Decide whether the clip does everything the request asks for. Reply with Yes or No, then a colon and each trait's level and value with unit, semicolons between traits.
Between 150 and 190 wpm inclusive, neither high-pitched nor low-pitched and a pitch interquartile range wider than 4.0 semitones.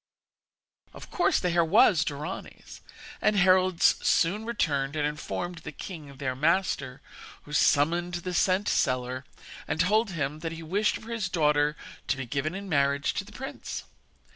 Yes: average, 160 wpm; medium, 165 Hz; average, 4.4 semitones